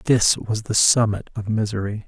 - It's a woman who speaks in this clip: No, male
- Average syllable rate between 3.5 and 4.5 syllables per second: No, 4.8 syllables/s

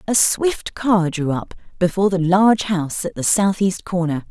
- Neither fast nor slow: Yes, average, 180 wpm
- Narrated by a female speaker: Yes, female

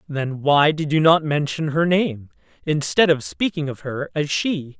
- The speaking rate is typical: Yes, average, 190 wpm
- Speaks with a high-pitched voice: No, medium, 150 Hz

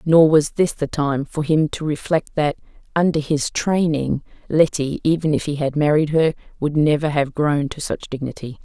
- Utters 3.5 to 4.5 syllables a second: No, 4.7 syllables/s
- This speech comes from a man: No, female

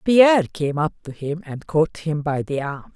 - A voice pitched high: No, medium, 160 Hz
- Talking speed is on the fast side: Yes, fast, 225 wpm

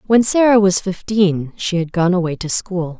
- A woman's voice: Yes, female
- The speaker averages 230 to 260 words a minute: No, average, 200 wpm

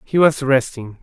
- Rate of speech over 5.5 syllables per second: No, 4.3 syllables/s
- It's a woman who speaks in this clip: No, male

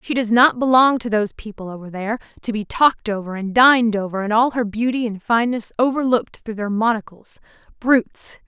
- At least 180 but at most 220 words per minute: Yes, average, 185 wpm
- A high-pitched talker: Yes, high, 225 Hz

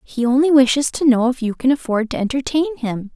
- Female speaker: Yes, female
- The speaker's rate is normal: No, fast, 230 wpm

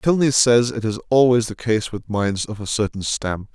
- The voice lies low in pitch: Yes, low, 115 Hz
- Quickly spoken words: Yes, fast, 220 wpm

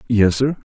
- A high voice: No, low, 115 Hz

